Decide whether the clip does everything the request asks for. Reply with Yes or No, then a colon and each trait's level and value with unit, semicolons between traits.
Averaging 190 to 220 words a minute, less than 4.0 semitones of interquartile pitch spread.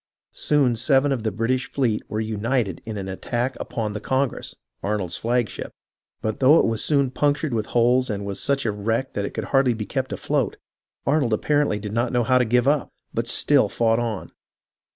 Yes: average, 200 wpm; average, 3.6 semitones